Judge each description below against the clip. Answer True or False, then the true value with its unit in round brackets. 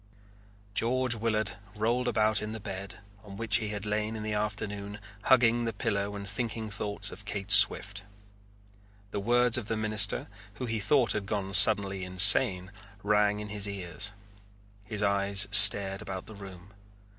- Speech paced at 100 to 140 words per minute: False (160 wpm)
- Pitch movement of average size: False (1.7 semitones)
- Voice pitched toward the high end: False (105 Hz)